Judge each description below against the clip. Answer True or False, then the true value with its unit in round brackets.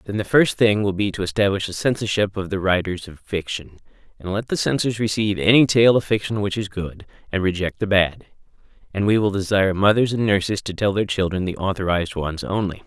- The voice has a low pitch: True (100 Hz)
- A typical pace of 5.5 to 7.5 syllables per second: True (5.9 syllables/s)